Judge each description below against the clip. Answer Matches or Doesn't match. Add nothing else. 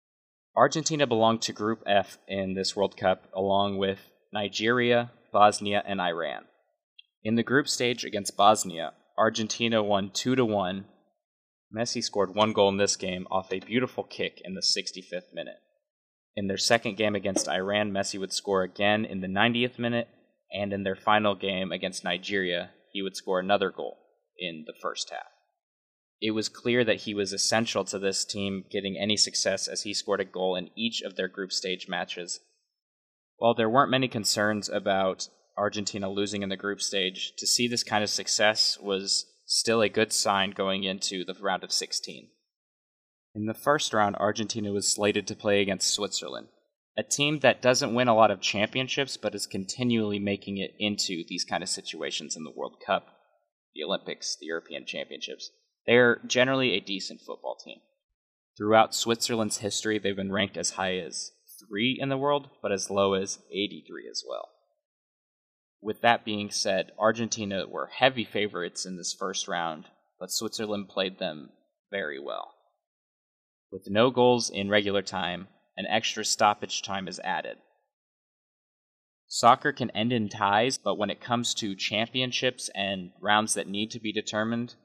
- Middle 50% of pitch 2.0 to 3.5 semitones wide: Matches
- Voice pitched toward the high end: Doesn't match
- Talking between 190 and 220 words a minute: Doesn't match